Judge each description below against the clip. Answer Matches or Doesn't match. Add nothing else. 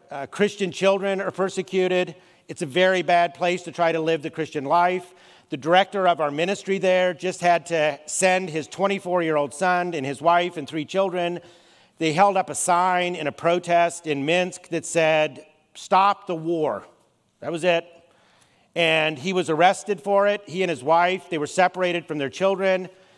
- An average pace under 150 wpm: Doesn't match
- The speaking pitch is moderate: Matches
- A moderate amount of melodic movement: Doesn't match